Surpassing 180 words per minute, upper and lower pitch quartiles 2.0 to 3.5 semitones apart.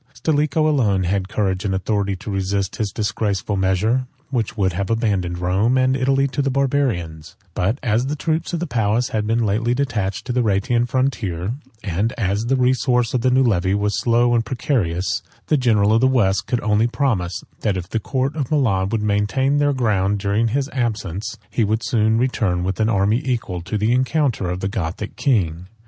No: average, 195 wpm; average, 4.7 semitones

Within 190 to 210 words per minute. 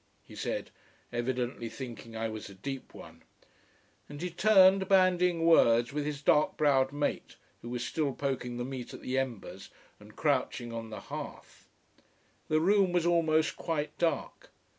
No: average, 160 wpm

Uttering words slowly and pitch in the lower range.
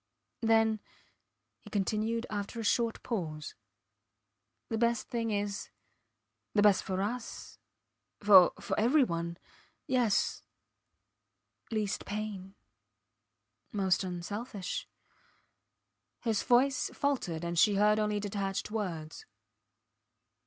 No: slow, 95 wpm; high, 210 Hz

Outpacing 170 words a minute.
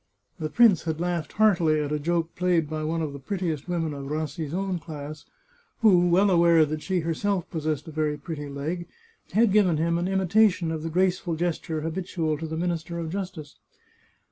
Yes: average, 195 wpm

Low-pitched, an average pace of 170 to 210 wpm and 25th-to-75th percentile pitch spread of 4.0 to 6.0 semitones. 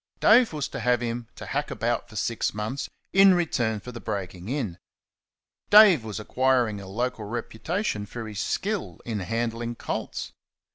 No: low, 120 Hz; average, 160 wpm; average, 4.6 semitones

